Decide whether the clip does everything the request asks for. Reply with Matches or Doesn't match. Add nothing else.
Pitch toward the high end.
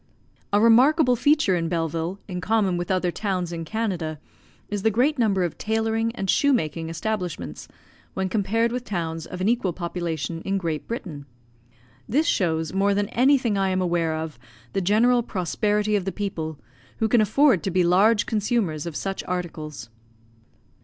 Matches